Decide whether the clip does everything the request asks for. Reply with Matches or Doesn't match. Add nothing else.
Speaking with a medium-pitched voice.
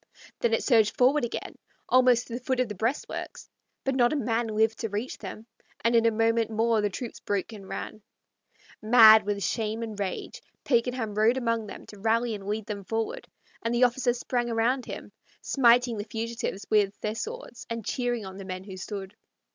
Doesn't match